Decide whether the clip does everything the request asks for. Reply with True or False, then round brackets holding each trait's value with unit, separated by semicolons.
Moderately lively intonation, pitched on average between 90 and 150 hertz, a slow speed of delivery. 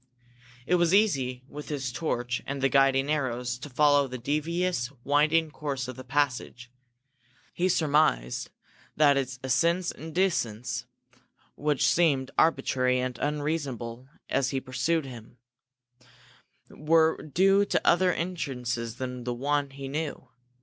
True (3.7 semitones; 140 Hz; 130 wpm)